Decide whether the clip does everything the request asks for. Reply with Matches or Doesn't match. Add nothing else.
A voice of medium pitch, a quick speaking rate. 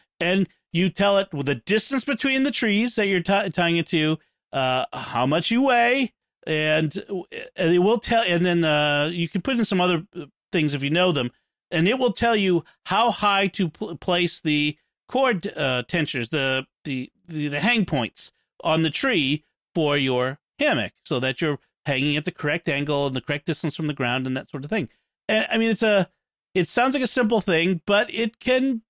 Matches